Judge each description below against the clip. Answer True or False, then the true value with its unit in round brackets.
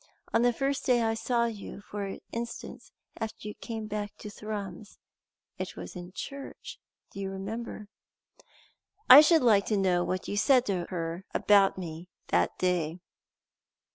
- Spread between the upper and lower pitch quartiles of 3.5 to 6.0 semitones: True (3.8 semitones)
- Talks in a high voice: True (205 Hz)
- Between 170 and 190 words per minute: False (155 wpm)